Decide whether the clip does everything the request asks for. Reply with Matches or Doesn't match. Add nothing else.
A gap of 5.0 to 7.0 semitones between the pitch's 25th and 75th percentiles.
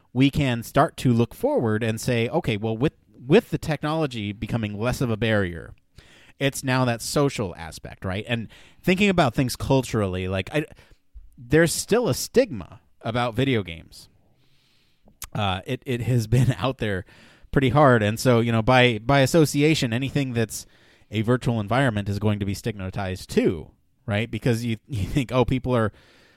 Doesn't match